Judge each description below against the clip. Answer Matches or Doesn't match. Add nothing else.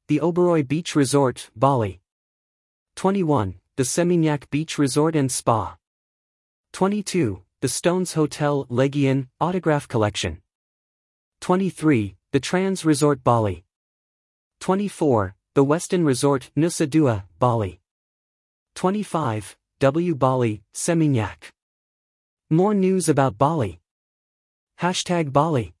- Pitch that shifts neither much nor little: Doesn't match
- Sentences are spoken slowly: Matches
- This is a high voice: Doesn't match